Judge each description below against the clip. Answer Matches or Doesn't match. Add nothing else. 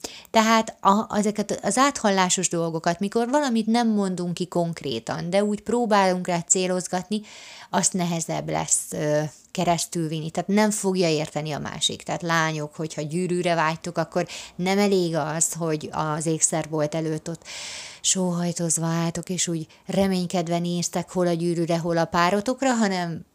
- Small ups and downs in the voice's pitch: Doesn't match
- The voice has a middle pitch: Matches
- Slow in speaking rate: Doesn't match